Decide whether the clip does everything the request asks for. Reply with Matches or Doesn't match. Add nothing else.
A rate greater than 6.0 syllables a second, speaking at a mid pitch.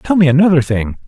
Matches